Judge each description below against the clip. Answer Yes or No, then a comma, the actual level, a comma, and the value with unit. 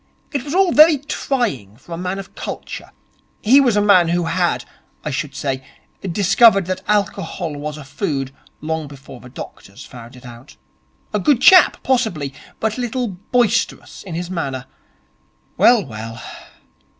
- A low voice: No, medium, 175 Hz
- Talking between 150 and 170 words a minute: Yes, average, 160 wpm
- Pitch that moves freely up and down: Yes, wide, 8.7 semitones